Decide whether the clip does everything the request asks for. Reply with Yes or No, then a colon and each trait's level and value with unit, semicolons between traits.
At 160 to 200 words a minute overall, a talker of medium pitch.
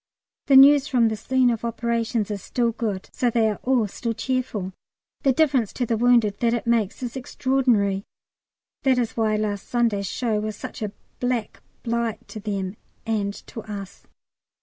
No: average, 170 wpm; high, 230 Hz